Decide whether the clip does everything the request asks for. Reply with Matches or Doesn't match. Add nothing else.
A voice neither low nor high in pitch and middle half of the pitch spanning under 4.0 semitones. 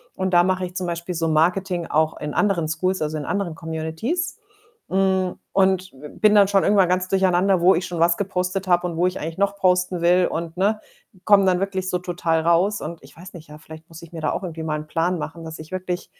Matches